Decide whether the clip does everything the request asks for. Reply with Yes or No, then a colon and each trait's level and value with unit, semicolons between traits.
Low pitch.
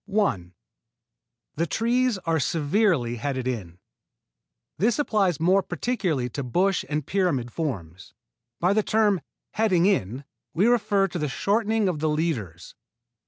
No: medium, 170 Hz